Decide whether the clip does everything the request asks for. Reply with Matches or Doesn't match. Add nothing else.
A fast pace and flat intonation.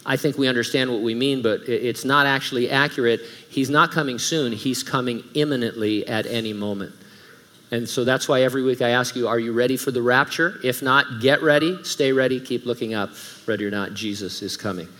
Doesn't match